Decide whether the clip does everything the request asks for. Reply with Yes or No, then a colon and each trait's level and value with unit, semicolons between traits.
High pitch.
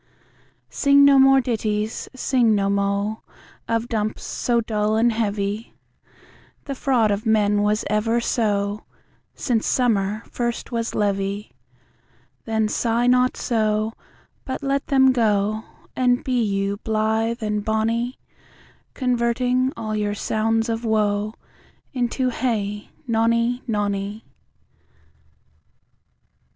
Yes: high, 220 Hz